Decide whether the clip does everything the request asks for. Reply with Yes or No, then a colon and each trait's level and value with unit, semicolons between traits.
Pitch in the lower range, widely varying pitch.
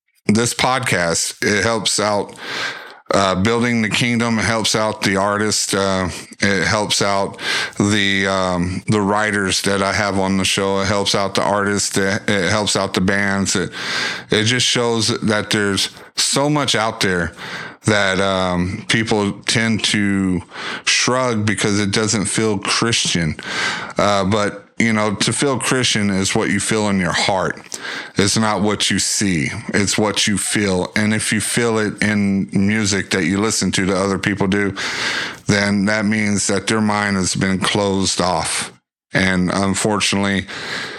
No: low, 100 Hz; narrow, 1.9 semitones